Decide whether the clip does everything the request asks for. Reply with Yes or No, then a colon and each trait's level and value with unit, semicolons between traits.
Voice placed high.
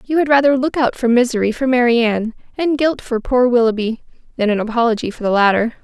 Yes: high, 240 Hz